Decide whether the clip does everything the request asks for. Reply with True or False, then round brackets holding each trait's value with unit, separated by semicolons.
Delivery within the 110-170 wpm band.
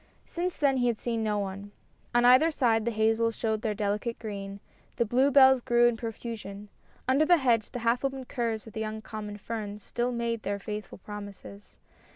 False (190 wpm)